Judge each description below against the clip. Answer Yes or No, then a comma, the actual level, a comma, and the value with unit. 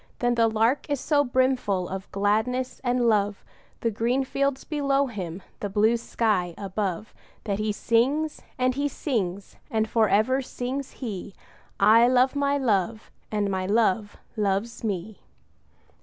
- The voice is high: Yes, high, 225 Hz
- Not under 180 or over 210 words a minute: No, average, 145 wpm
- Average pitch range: Yes, average, 4.1 semitones